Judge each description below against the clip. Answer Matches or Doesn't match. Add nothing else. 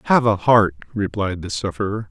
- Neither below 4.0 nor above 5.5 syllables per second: Matches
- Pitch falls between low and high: Doesn't match